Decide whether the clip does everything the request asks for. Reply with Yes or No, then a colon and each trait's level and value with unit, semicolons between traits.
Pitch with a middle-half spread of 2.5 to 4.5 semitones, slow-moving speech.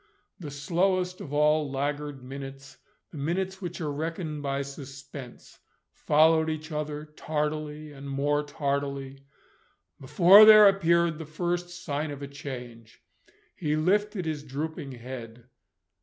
Yes: average, 3.1 semitones; slow, 125 wpm